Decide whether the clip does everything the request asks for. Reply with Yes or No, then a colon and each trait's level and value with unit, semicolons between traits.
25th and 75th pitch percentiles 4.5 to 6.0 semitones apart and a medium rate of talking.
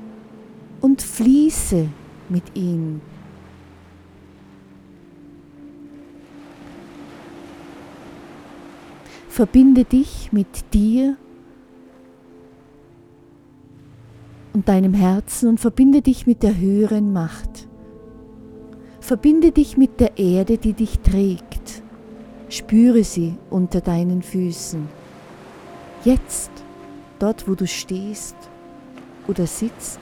No: wide, 5.4 semitones; slow, 75 wpm